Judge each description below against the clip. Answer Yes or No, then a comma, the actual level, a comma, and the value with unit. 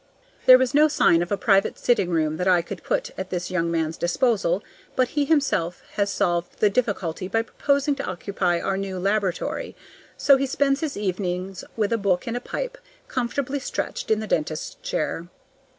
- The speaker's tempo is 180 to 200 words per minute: Yes, average, 185 wpm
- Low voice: No, high, 200 Hz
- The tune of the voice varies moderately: No, wide, 6.4 semitones